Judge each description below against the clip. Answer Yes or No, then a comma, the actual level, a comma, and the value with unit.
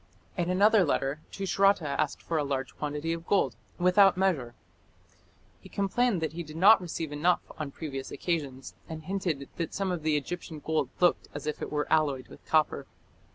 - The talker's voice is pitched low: No, medium, 160 Hz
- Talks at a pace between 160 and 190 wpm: Yes, average, 180 wpm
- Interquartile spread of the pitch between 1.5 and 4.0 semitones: Yes, average, 3.7 semitones